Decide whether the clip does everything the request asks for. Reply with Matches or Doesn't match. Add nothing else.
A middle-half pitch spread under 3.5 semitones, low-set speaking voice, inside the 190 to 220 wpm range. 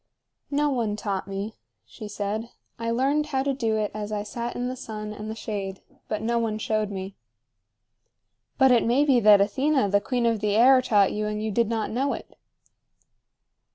Doesn't match